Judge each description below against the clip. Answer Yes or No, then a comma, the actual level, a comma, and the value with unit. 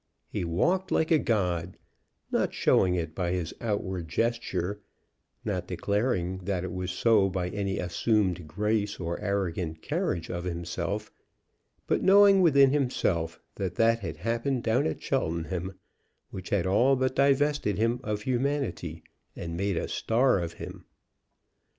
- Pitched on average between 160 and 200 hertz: No, low, 100 Hz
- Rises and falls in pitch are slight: No, average, 5.1 semitones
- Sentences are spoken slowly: No, average, 145 wpm